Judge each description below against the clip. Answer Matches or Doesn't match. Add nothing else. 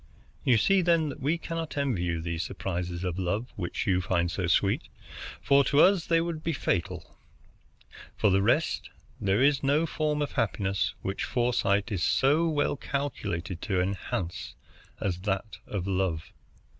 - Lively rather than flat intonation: Matches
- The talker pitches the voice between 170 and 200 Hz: Doesn't match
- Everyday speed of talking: Matches